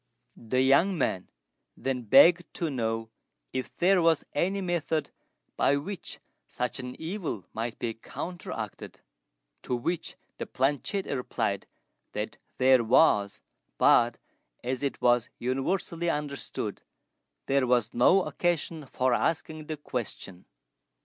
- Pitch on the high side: No, low, 135 Hz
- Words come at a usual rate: No, slow, 120 wpm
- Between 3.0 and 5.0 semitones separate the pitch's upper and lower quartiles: No, wide, 5.5 semitones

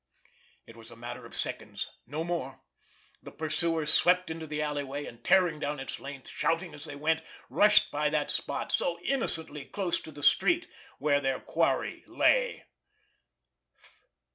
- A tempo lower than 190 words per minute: Yes, average, 150 wpm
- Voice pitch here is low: No, medium, 150 Hz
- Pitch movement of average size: Yes, average, 3.0 semitones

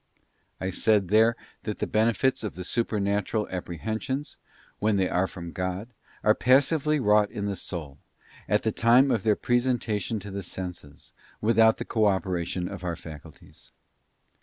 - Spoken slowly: No, average, 150 wpm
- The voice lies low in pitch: Yes, low, 105 Hz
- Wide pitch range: No, average, 3.9 semitones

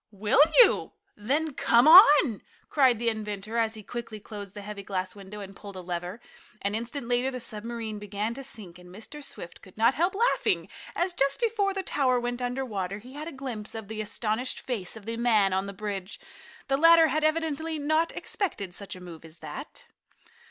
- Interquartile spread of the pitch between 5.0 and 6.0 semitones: Yes, wide, 5.4 semitones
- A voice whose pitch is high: Yes, high, 230 Hz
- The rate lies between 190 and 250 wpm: Yes, average, 200 wpm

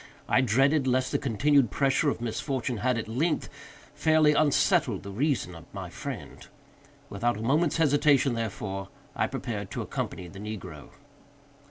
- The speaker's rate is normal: Yes, average, 150 wpm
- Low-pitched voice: Yes, low, 125 Hz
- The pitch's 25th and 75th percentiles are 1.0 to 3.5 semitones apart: No, average, 5.2 semitones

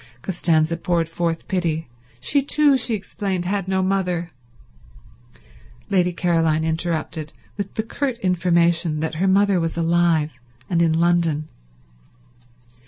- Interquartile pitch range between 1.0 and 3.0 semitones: Yes, average, 2.7 semitones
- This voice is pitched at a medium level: Yes, medium, 175 Hz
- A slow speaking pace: Yes, slow, 120 wpm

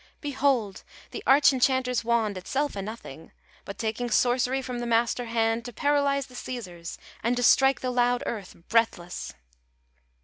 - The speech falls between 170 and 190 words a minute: No, average, 150 wpm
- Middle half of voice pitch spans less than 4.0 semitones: Yes, narrow, 2.6 semitones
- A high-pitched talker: Yes, high, 245 Hz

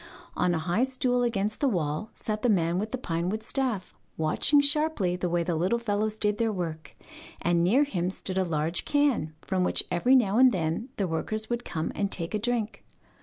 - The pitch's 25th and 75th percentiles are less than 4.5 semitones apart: No, wide, 5.6 semitones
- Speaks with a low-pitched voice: No, high, 205 Hz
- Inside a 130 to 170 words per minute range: No, fast, 205 wpm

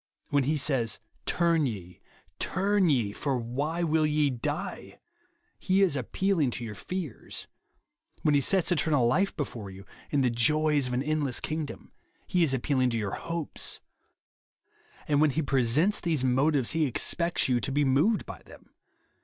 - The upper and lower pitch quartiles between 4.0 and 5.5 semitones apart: Yes, average, 4.4 semitones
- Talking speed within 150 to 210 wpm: Yes, average, 170 wpm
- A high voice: No, medium, 145 Hz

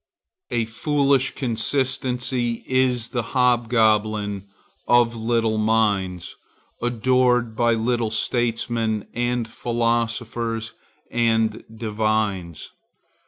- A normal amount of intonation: No, narrow, 1.8 semitones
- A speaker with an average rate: No, slow, 75 wpm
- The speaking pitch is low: Yes, low, 115 Hz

